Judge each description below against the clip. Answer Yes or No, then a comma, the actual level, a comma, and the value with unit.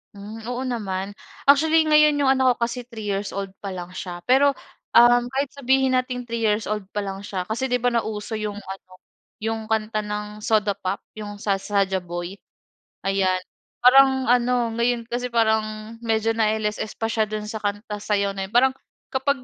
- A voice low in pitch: No, high, 220 Hz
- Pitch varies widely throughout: No, average, 3.4 semitones